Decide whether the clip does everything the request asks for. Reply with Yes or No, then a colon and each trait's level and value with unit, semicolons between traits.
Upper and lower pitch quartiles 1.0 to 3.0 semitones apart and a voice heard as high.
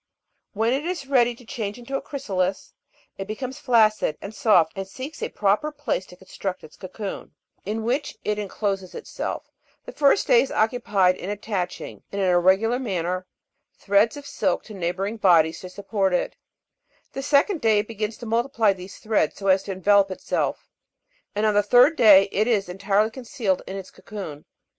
No: average, 3.9 semitones; high, 210 Hz